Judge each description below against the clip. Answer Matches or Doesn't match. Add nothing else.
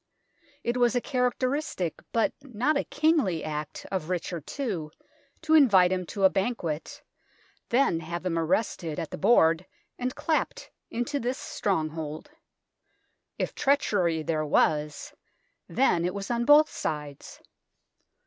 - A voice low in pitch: Doesn't match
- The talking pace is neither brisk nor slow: Doesn't match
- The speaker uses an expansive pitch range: Matches